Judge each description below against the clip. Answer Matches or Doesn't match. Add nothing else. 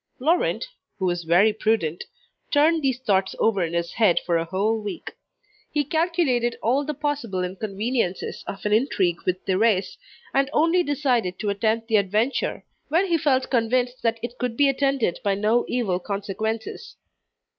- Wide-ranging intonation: Matches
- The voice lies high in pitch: Matches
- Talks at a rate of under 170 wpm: Matches